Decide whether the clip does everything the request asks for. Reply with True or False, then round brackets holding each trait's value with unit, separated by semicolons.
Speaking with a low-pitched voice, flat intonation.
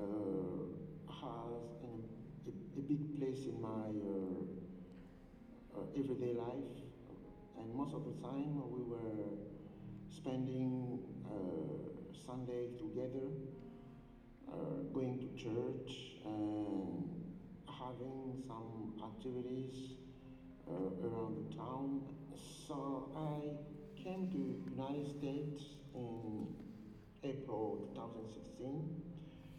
False (130 Hz; 4.1 semitones)